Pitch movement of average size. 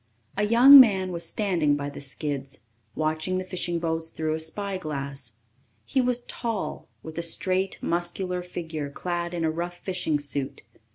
Yes: average, 3.2 semitones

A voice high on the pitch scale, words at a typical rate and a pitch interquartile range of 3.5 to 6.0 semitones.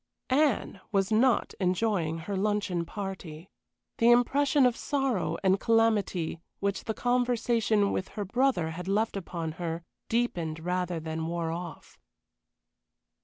No: high, 195 Hz; slow, 125 wpm; average, 5.1 semitones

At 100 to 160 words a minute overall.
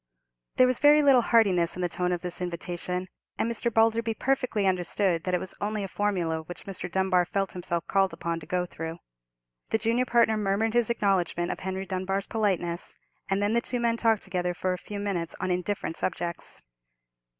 No: average, 195 wpm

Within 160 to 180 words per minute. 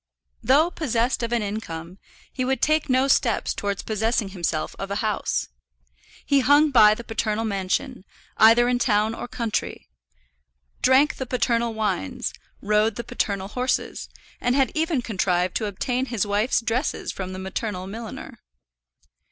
No: average, 150 wpm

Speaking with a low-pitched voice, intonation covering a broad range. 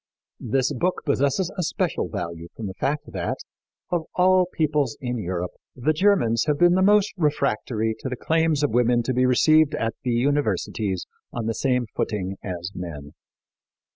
Yes: low, 130 Hz; wide, 6.2 semitones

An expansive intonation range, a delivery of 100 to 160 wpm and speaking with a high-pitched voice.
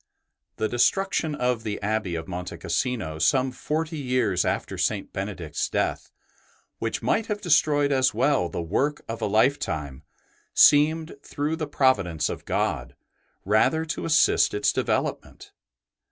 No: wide, 7.3 semitones; average, 140 wpm; low, 125 Hz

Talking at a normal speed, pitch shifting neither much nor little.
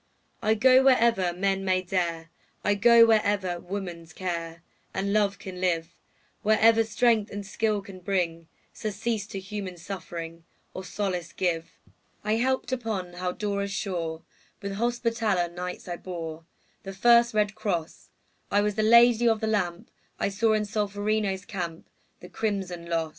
Yes: average, 145 wpm; average, 3.5 semitones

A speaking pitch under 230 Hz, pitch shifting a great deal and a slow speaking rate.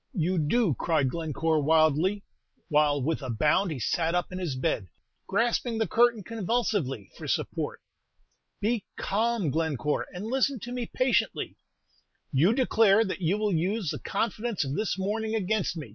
No: medium, 185 Hz; wide, 6.1 semitones; average, 160 wpm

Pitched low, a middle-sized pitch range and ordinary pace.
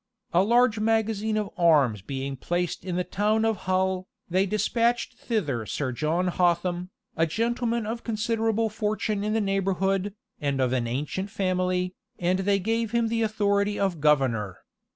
No: high, 195 Hz; average, 4.2 semitones; average, 155 wpm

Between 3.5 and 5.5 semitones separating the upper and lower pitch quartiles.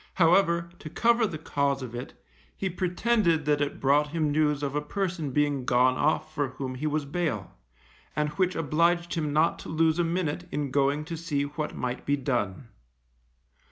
No: average, 3.1 semitones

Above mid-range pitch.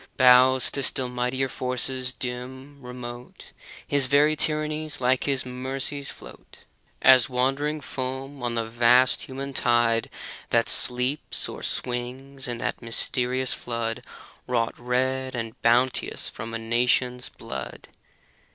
No: low, 125 Hz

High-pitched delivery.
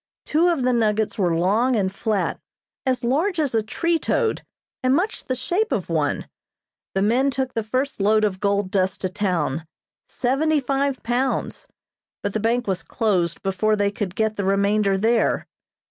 Yes: high, 220 Hz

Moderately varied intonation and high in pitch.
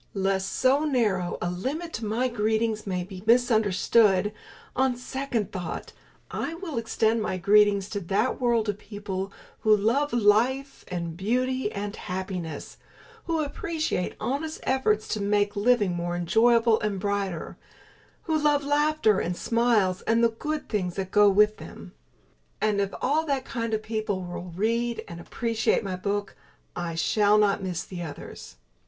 Yes: average, 4.1 semitones; high, 210 Hz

